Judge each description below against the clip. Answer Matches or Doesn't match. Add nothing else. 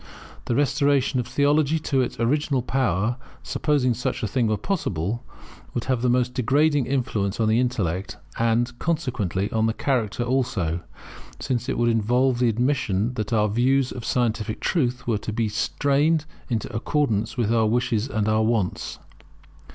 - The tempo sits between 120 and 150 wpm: Doesn't match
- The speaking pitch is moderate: Doesn't match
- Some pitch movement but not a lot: Matches